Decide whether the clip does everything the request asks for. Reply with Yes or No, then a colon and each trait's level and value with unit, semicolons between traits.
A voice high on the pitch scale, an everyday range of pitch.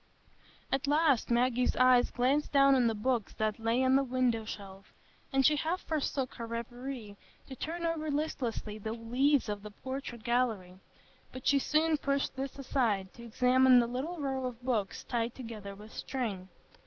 Yes: very high, 250 Hz; average, 3.3 semitones